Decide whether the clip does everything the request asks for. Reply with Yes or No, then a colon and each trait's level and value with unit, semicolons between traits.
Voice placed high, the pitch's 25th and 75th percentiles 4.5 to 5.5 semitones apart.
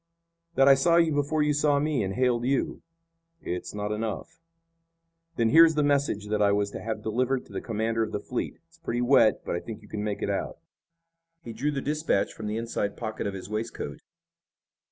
No: low, 115 Hz; average, 5.2 semitones